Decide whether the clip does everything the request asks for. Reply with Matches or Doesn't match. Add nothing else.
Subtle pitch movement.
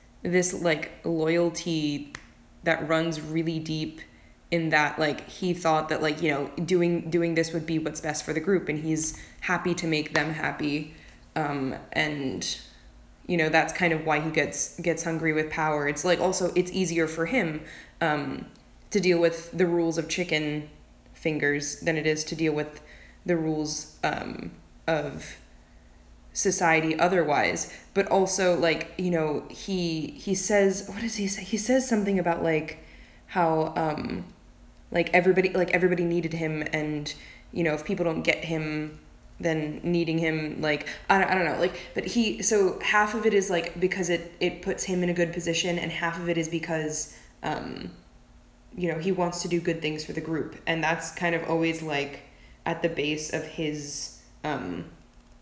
Matches